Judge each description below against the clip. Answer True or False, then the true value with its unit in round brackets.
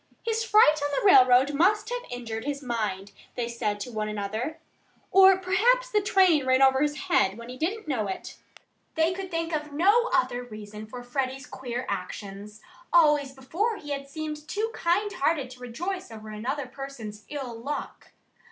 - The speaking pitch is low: False (275 Hz)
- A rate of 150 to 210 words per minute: True (175 wpm)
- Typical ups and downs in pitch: False (6.8 semitones)